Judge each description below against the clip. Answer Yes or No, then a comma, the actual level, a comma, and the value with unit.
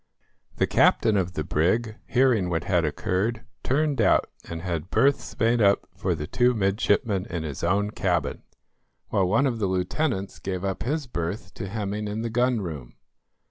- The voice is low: Yes, low, 100 Hz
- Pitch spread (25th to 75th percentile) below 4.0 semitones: No, average, 4.3 semitones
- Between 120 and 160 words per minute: No, average, 175 wpm